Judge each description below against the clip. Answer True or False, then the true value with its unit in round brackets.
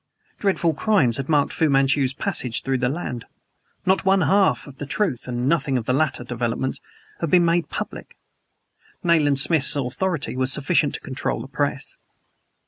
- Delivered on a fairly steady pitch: False (4.6 semitones)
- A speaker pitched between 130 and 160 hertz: True (140 Hz)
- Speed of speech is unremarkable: True (165 wpm)